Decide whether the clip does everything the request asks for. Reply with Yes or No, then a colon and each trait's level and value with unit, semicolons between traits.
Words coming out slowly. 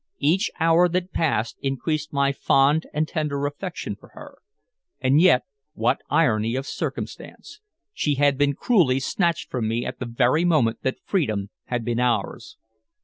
No: average, 155 wpm